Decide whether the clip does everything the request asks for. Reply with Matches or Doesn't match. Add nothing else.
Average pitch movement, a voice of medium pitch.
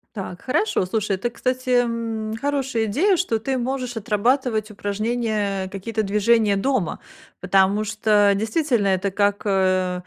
Doesn't match